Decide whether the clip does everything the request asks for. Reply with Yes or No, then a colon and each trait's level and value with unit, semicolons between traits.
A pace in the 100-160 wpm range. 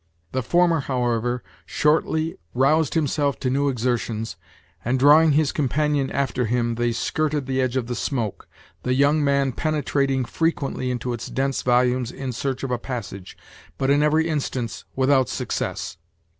Yes: average, 155 wpm